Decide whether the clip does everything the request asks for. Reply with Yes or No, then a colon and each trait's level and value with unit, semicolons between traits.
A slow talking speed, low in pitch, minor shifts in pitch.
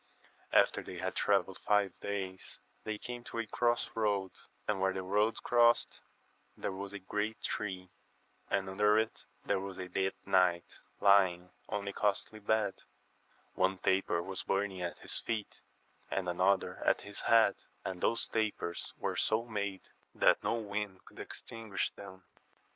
No: average, 155 wpm; low, 100 Hz; narrow, 2.3 semitones